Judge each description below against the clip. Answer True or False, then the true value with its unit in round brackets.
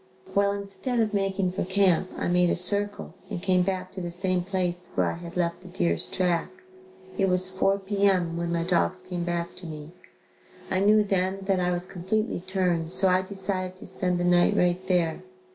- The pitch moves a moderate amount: False (1.7 semitones)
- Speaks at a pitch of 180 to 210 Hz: True (185 Hz)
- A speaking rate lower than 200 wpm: False (205 wpm)